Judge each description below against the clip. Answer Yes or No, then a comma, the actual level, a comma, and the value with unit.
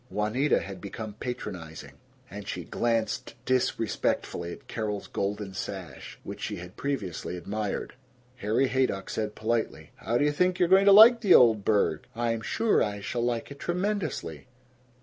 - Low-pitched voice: Yes, low, 110 Hz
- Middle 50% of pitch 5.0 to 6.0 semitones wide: Yes, average, 5.3 semitones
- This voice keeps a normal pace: Yes, average, 155 wpm